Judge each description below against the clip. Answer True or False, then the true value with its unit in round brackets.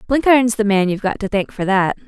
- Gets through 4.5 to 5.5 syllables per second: False (6.4 syllables/s)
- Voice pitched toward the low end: False (210 Hz)